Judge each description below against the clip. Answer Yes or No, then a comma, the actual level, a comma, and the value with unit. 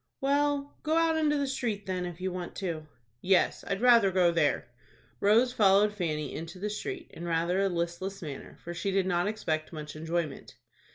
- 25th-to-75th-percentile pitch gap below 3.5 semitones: No, average, 4.5 semitones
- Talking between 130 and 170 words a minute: No, average, 185 wpm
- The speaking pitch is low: No, high, 190 Hz